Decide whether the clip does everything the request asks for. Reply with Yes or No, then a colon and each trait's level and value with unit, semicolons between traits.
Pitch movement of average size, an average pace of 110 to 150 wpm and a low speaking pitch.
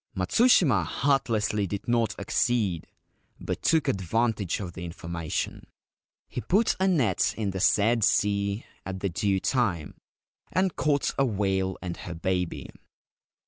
Yes: average, 4.4 semitones; slow, 135 wpm; low, 100 Hz